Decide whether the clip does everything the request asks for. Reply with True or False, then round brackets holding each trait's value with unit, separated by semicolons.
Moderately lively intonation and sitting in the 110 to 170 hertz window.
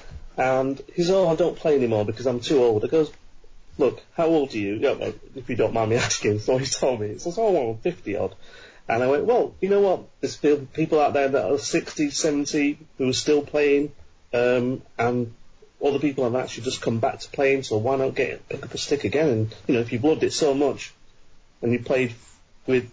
True (3.9 semitones; 135 Hz)